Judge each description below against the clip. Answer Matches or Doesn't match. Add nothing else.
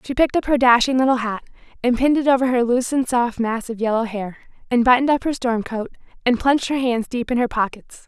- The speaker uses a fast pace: Matches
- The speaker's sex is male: Doesn't match